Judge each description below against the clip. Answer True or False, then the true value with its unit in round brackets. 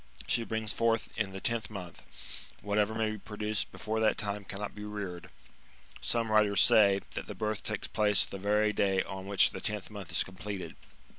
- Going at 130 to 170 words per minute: False (190 wpm)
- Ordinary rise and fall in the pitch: False (1.6 semitones)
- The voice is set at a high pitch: False (105 Hz)